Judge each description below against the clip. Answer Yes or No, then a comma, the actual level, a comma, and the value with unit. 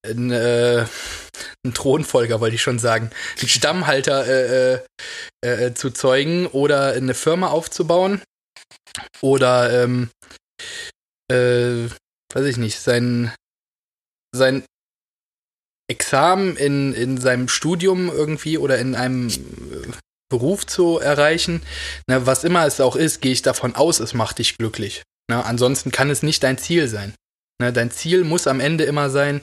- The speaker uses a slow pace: No, average, 135 wpm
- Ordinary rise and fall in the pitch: Yes, average, 3.4 semitones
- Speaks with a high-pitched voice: No, low, 130 Hz